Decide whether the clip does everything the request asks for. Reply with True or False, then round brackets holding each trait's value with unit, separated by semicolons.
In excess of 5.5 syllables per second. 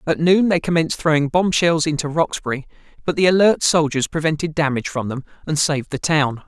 True (6.0 syllables/s)